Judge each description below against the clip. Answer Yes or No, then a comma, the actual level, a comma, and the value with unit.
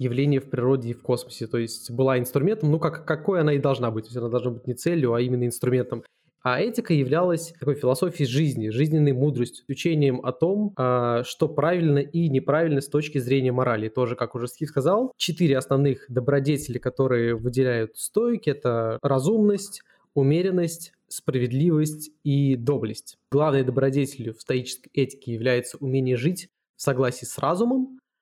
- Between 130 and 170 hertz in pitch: Yes, low, 135 Hz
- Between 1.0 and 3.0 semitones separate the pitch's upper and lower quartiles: No, average, 4.2 semitones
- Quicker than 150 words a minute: Yes, fast, 160 wpm